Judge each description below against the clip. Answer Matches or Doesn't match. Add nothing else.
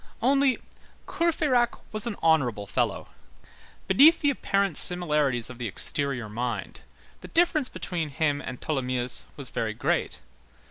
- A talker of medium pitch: Matches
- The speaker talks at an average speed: Doesn't match